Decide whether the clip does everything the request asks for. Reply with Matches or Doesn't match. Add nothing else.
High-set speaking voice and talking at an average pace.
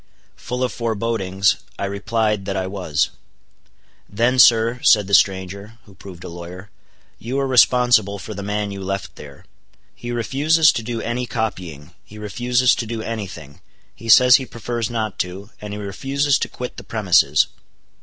Doesn't match